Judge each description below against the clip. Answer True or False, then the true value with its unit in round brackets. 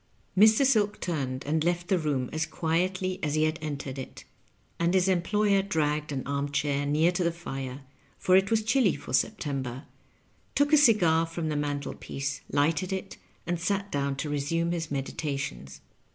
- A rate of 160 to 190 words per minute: True (170 wpm)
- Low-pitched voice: False (160 Hz)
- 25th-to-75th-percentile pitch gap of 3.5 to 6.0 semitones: True (4.6 semitones)